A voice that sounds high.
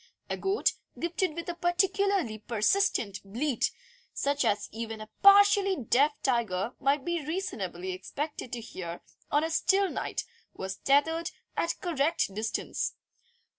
Yes: very high, 285 Hz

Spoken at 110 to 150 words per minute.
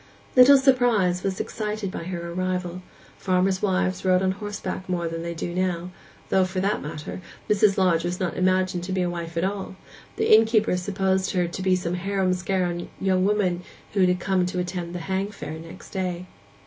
No: average, 185 wpm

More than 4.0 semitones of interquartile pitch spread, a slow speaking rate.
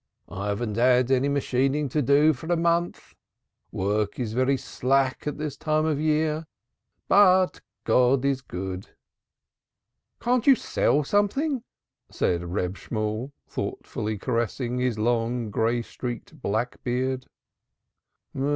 Yes: average, 5.0 semitones; slow, 125 wpm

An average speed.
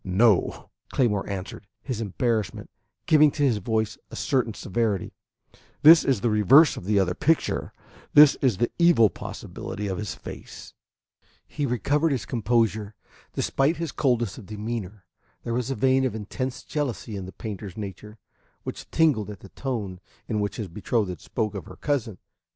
Yes: average, 160 wpm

